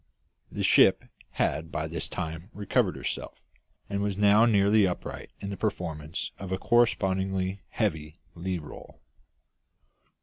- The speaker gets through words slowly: Yes, slow, 130 wpm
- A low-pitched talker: Yes, very low, 95 Hz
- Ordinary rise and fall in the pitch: Yes, average, 3.5 semitones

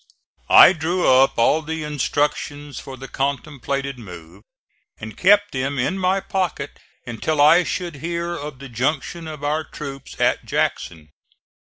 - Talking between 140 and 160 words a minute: Yes, average, 145 wpm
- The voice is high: No, medium, 145 Hz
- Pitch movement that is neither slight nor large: Yes, average, 3.6 semitones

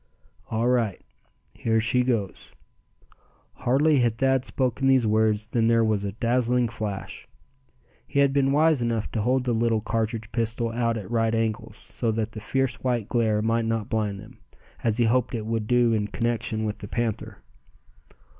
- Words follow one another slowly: No, average, 175 wpm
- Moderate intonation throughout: No, narrow, 2.0 semitones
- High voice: No, low, 115 Hz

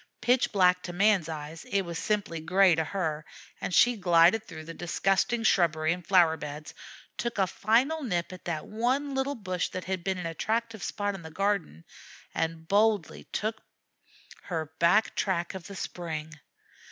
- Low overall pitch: No, medium, 185 Hz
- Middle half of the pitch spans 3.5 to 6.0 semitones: Yes, average, 4.3 semitones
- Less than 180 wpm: Yes, average, 170 wpm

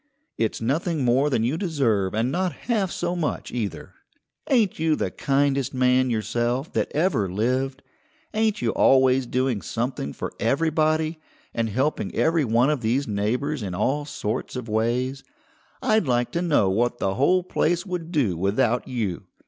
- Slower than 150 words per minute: No, average, 160 wpm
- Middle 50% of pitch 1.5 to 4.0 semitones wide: No, average, 5.3 semitones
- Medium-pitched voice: No, low, 130 Hz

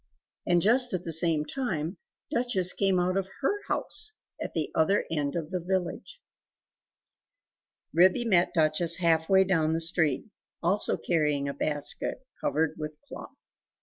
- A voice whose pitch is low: No, medium, 175 Hz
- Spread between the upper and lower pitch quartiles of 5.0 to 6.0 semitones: No, average, 3.4 semitones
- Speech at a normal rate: Yes, average, 150 wpm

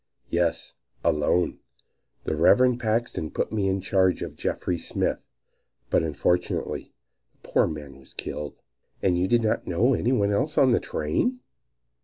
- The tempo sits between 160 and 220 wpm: No, average, 150 wpm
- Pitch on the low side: Yes, very low, 95 Hz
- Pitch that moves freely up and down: Yes, wide, 6.6 semitones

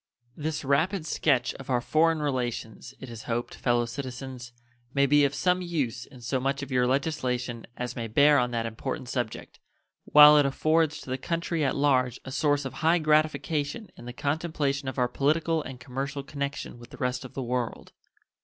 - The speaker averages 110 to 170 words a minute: No, average, 190 wpm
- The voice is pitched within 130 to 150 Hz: Yes, low, 135 Hz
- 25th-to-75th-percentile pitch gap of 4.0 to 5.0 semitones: No, average, 3.3 semitones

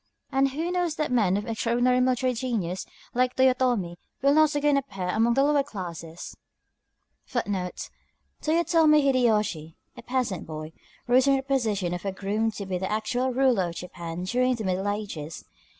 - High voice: Yes, high, 235 Hz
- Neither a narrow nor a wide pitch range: No, wide, 6.0 semitones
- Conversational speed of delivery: Yes, average, 160 wpm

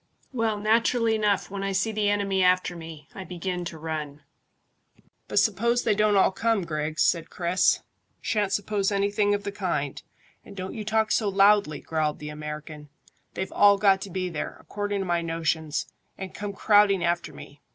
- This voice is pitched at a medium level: No, high, 195 Hz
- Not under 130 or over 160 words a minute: No, average, 180 wpm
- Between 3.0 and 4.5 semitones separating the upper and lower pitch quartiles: Yes, average, 3.8 semitones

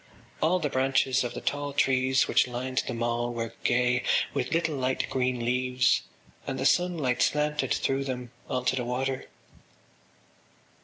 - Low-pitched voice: Yes, low, 130 Hz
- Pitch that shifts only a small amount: Yes, narrow, 1.5 semitones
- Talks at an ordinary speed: Yes, average, 155 wpm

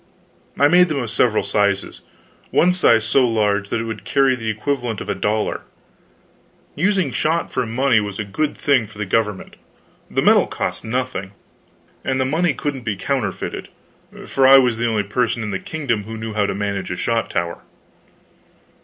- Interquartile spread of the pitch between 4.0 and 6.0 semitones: Yes, average, 4.6 semitones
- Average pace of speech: Yes, average, 180 wpm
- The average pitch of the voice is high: No, low, 115 Hz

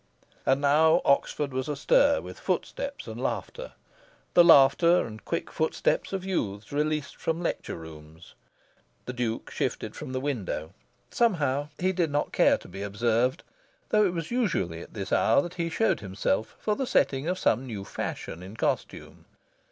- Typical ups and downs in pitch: No, wide, 7.8 semitones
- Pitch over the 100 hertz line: Yes, medium, 140 Hz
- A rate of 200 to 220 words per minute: No, average, 165 wpm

